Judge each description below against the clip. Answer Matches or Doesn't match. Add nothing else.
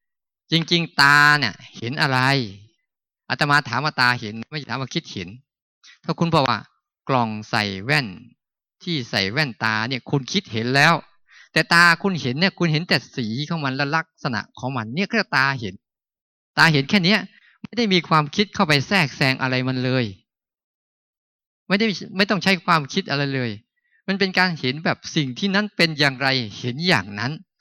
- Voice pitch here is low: Doesn't match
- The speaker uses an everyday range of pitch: Doesn't match